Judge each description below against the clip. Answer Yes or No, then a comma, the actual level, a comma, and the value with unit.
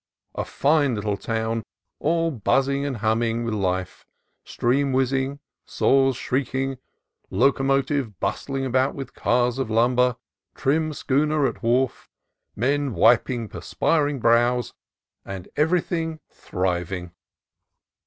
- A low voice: Yes, low, 130 Hz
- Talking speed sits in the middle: No, slow, 110 wpm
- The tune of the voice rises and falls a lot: No, average, 3.4 semitones